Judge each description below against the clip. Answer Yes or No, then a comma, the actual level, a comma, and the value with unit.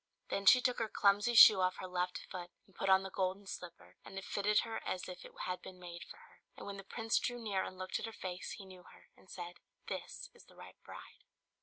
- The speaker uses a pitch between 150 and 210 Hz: Yes, high, 190 Hz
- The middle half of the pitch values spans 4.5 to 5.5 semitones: No, narrow, 2.4 semitones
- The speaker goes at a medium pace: No, fast, 255 wpm